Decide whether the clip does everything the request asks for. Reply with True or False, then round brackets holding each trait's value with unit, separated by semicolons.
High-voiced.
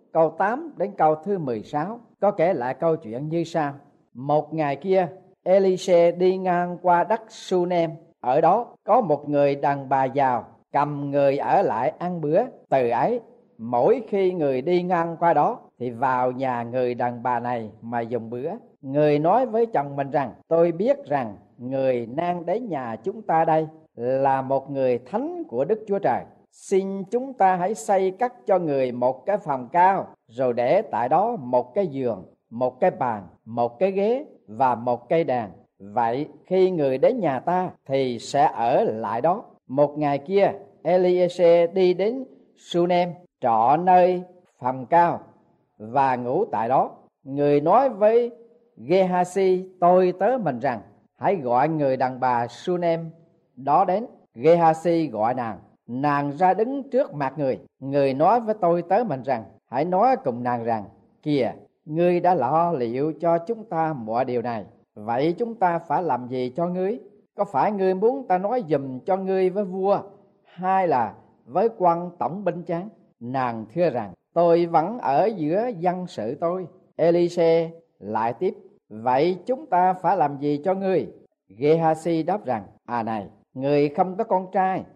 False (170 Hz)